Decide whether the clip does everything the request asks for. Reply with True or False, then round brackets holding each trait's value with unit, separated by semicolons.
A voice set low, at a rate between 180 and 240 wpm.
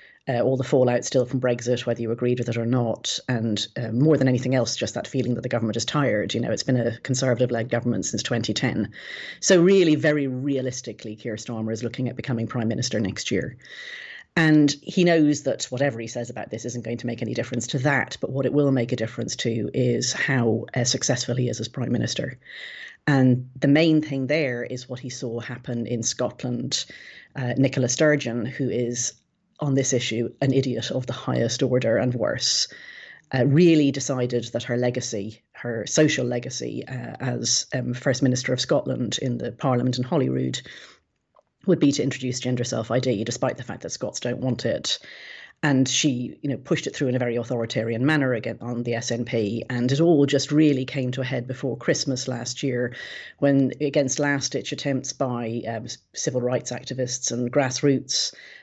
True (125 Hz; 195 wpm)